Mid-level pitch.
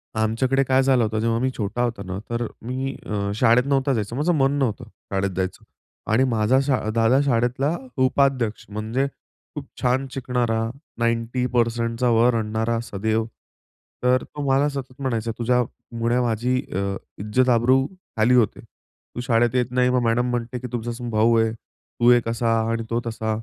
No: low, 120 Hz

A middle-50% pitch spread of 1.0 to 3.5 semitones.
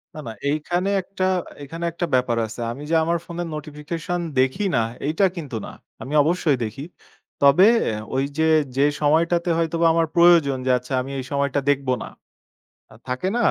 No: average, 4.0 semitones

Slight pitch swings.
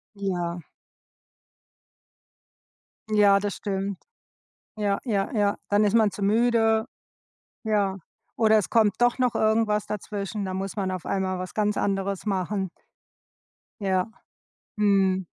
Yes: narrow, 2.0 semitones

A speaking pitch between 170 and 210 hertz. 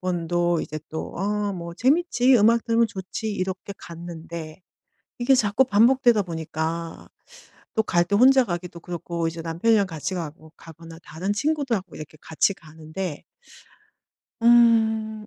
Yes: medium, 185 Hz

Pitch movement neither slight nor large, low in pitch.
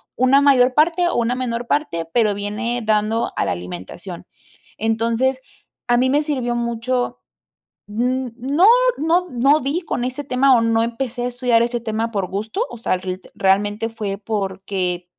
No: average, 3.5 semitones; high, 235 Hz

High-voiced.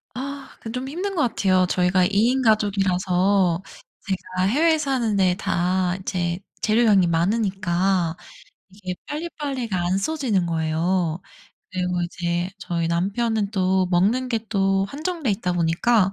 Yes: high, 195 Hz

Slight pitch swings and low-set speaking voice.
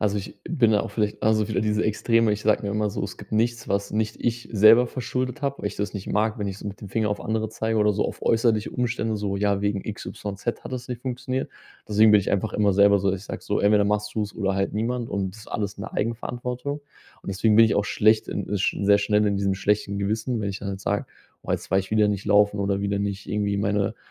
Yes: narrow, 1.7 semitones; low, 105 Hz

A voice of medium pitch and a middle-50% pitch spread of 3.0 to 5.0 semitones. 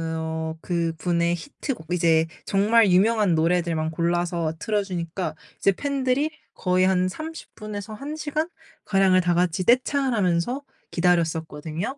Yes: medium, 180 Hz; average, 4.7 semitones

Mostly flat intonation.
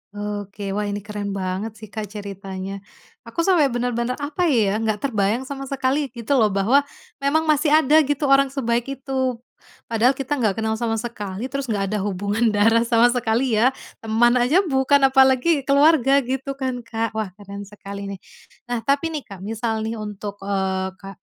No: average, 4.7 semitones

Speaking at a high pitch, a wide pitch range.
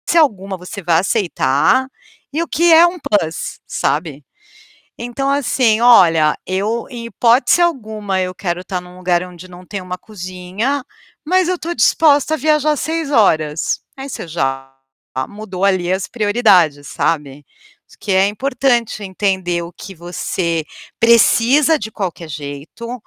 Yes: high, 200 Hz; wide, 6.3 semitones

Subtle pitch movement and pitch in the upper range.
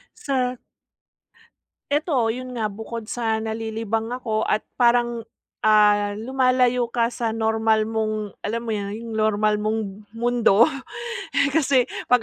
Yes: narrow, 2.3 semitones; high, 225 Hz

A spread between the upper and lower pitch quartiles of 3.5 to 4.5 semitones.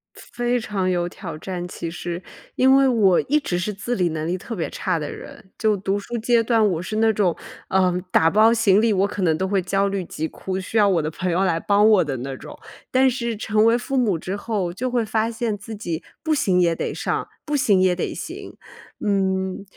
Yes: average, 3.9 semitones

